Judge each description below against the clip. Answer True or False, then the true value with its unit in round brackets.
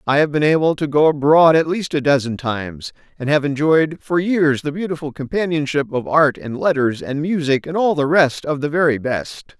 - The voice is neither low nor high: True (150 Hz)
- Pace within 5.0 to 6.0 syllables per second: True (5.2 syllables/s)